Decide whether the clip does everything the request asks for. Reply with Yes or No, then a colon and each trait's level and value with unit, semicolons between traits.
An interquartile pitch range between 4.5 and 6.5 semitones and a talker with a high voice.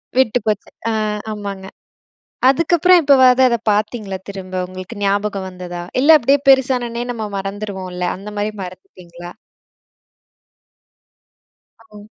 Yes: average, 4.8 semitones; high, 210 Hz